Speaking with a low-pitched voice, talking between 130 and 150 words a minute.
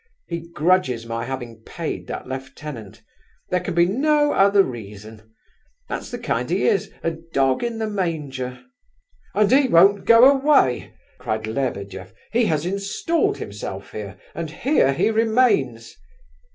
No: medium, 155 Hz; average, 140 wpm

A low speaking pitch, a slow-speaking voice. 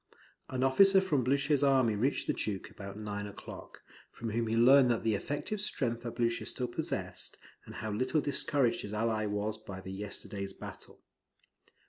No: low, 115 Hz; average, 165 wpm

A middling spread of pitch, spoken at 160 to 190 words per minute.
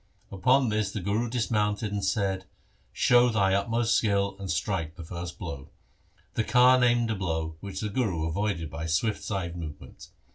Yes: average, 4.6 semitones; average, 180 wpm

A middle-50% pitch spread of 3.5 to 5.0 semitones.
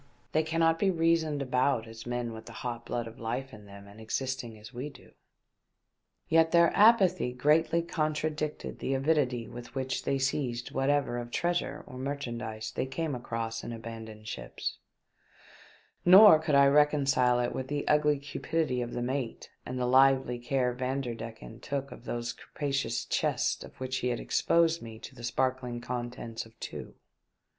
Yes: average, 3.8 semitones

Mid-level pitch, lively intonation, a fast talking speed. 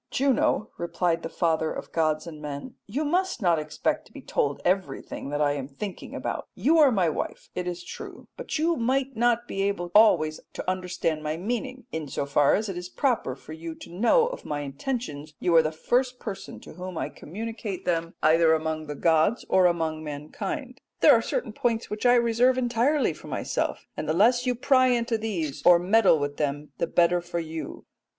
Yes: medium, 180 Hz; wide, 7.2 semitones; fast, 210 wpm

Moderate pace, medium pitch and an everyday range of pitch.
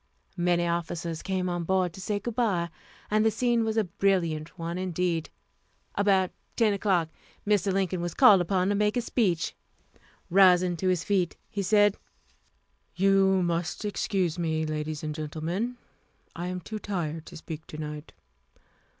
Yes: average, 160 wpm; medium, 180 Hz; average, 3.2 semitones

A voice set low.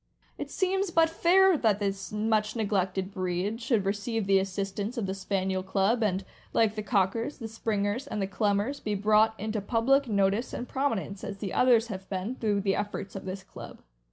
No: high, 210 Hz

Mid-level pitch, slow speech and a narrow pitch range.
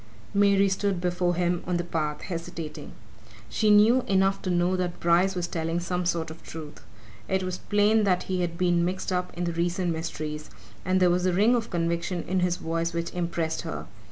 No: medium, 175 Hz; average, 200 wpm; narrow, 1.9 semitones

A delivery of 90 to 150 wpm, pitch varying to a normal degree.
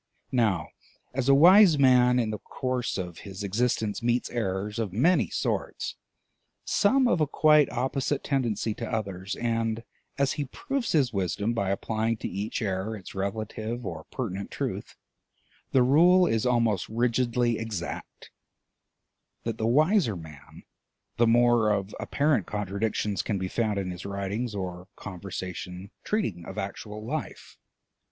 Yes: average, 145 wpm; average, 4.2 semitones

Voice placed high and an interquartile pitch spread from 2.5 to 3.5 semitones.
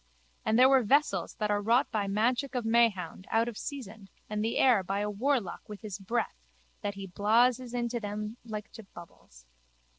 Yes: high, 220 Hz; average, 3.0 semitones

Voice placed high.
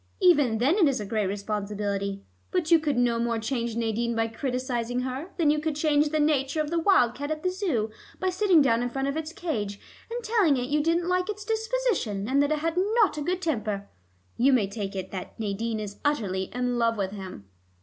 Yes: very high, 260 Hz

